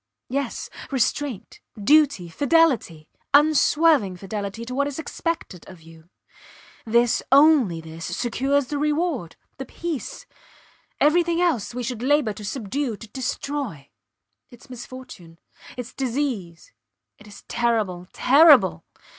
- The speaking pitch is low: No, very high, 250 Hz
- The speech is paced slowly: Yes, slow, 115 wpm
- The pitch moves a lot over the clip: Yes, wide, 6.5 semitones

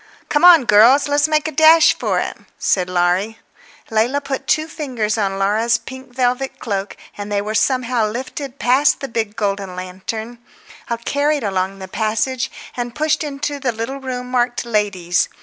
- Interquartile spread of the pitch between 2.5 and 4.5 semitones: No, average, 5.0 semitones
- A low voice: No, high, 240 Hz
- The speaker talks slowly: No, average, 165 wpm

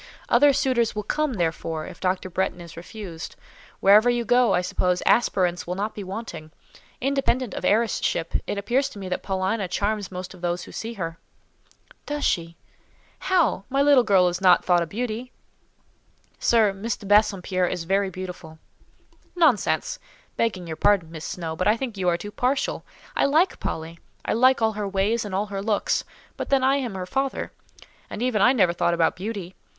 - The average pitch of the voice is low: No, high, 200 Hz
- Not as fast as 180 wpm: No, average, 185 wpm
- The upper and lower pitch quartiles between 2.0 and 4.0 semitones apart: No, average, 4.7 semitones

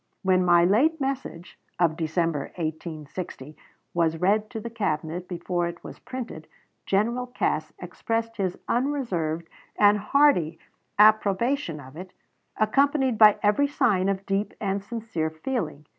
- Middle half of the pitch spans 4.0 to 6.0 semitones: Yes, wide, 5.5 semitones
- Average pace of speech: No, slow, 130 wpm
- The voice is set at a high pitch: Yes, high, 195 Hz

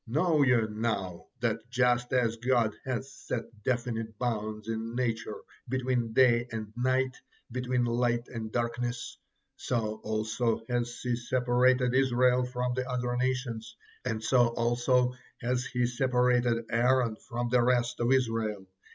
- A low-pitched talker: Yes, low, 120 Hz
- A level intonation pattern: Yes, narrow, 1.7 semitones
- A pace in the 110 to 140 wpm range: Yes, slow, 135 wpm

